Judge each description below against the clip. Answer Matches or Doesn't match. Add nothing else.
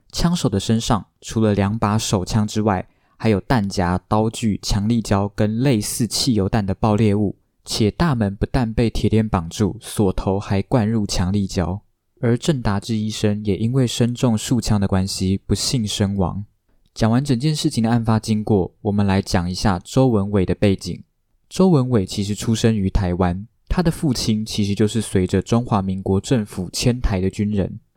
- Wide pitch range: Doesn't match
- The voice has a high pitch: Doesn't match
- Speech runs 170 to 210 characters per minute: Doesn't match